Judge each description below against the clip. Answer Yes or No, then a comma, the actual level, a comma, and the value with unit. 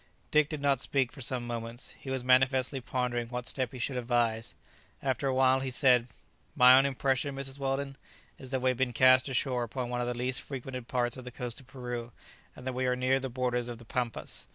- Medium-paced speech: No, fast, 225 wpm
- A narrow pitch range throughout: Yes, narrow, 1.5 semitones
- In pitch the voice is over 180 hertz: No, low, 130 Hz